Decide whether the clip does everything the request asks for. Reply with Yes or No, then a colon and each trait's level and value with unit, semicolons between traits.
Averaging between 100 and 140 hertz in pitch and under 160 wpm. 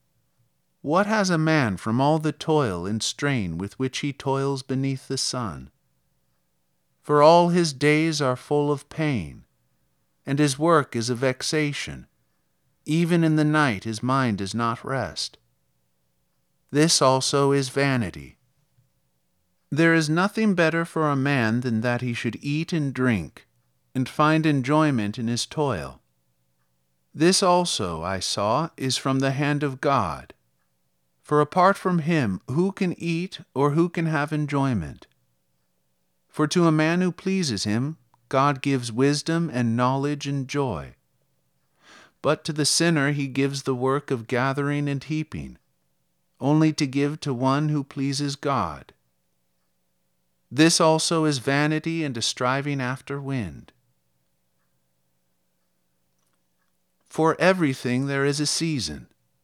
Yes: low, 135 Hz; slow, 135 wpm